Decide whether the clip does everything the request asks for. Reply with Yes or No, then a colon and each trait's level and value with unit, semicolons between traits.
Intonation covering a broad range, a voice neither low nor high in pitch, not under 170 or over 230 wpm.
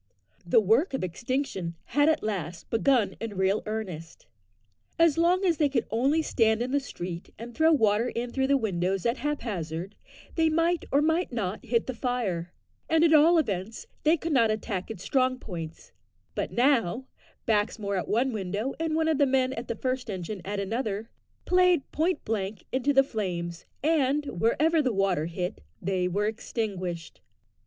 No: wide, 6.5 semitones; high, 230 Hz; average, 175 wpm